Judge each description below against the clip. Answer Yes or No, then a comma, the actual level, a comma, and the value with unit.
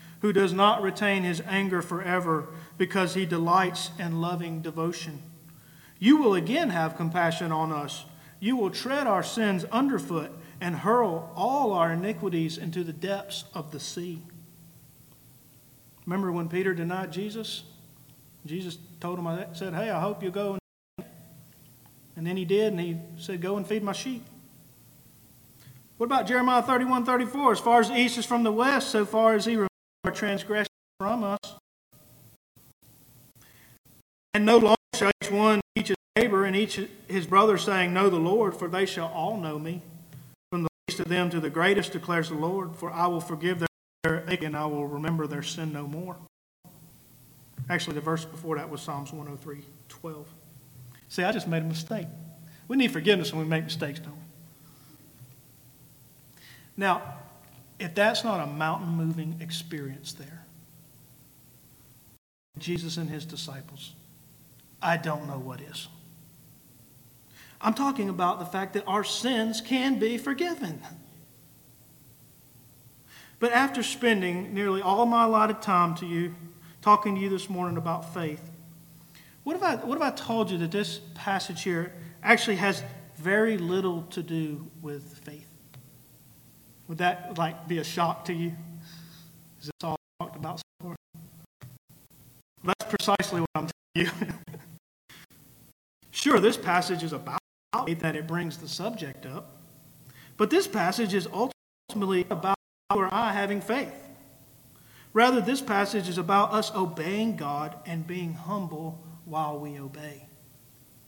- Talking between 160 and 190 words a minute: No, average, 150 wpm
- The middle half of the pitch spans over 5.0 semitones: No, average, 4.6 semitones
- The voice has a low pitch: No, medium, 170 Hz